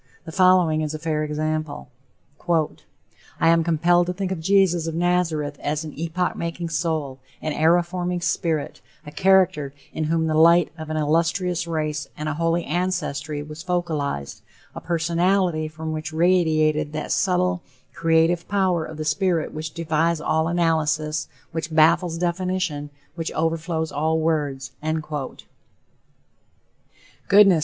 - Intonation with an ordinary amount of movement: No, narrow, 2.1 semitones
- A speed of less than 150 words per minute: Yes, average, 140 wpm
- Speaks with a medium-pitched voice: Yes, medium, 160 Hz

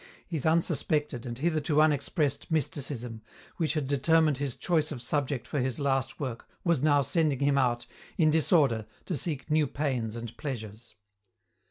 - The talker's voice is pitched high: No, medium, 140 Hz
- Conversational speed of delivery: Yes, average, 155 wpm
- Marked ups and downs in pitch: No, average, 3.5 semitones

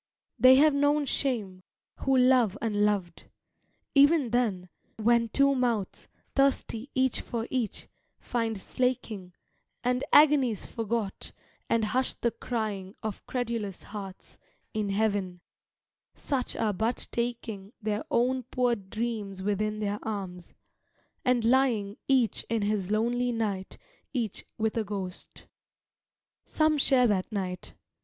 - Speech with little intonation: No, average, 3.7 semitones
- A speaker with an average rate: No, slow, 120 wpm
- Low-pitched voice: No, high, 225 Hz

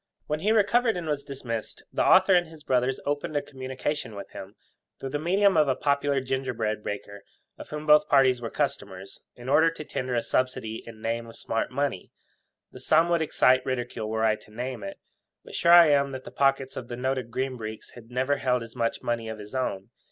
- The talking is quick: Yes, fast, 215 wpm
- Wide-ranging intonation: No, average, 4.2 semitones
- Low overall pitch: Yes, low, 130 Hz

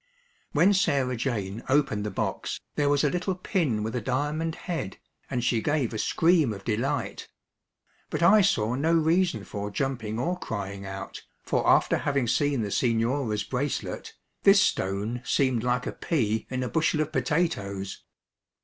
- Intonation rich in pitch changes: Yes, wide, 6.1 semitones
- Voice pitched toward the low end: Yes, low, 130 Hz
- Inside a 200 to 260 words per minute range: No, average, 160 wpm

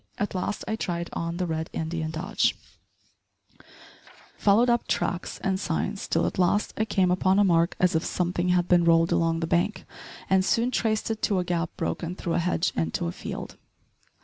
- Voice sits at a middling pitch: Yes, medium, 180 Hz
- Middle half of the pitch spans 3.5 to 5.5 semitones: No, average, 2.9 semitones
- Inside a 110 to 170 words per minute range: No, average, 190 wpm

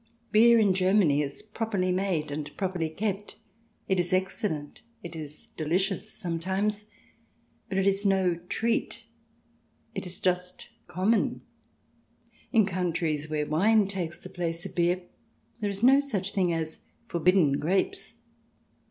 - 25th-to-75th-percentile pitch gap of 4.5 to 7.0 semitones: No, average, 3.3 semitones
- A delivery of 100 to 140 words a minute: Yes, slow, 135 wpm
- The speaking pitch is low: No, medium, 185 Hz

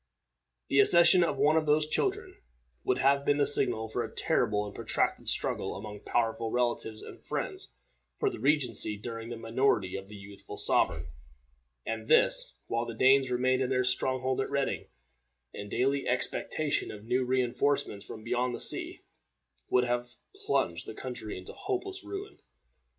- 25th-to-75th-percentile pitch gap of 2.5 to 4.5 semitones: Yes, average, 3.9 semitones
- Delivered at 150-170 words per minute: Yes, average, 165 wpm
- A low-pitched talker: Yes, low, 125 Hz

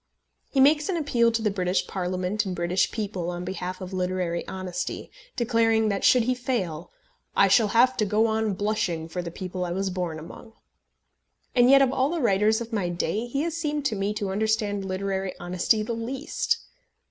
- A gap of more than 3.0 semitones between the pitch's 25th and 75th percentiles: Yes, average, 4.2 semitones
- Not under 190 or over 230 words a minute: Yes, average, 195 wpm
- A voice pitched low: No, high, 205 Hz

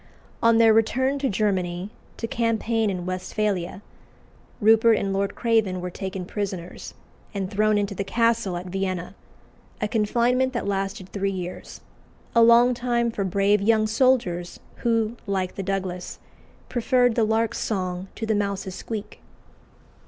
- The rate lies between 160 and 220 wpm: No, average, 145 wpm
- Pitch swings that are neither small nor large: Yes, average, 3.3 semitones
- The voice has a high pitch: Yes, high, 205 Hz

